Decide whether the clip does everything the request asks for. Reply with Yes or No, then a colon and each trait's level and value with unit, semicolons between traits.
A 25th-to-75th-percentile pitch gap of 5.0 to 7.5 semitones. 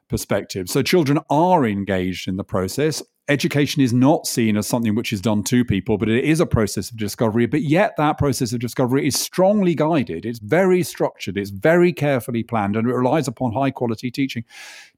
Yes: average, 5.3 semitones